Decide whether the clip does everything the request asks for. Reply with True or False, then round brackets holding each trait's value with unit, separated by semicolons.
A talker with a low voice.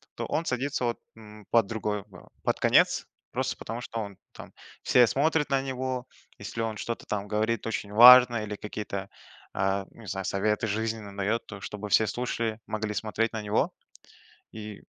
True (110 Hz)